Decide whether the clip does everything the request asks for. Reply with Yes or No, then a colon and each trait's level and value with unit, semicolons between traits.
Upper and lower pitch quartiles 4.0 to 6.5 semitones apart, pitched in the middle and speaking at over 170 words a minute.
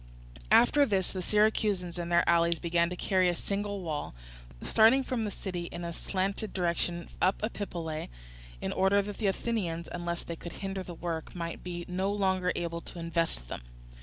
No: average, 2.9 semitones; medium, 180 Hz; average, 180 wpm